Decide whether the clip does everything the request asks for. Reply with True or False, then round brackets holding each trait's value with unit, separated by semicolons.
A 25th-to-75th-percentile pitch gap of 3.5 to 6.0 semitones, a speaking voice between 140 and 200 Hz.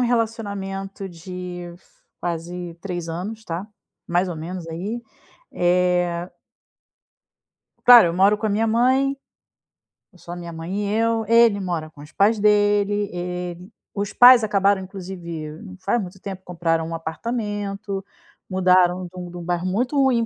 False (3.0 semitones; 190 Hz)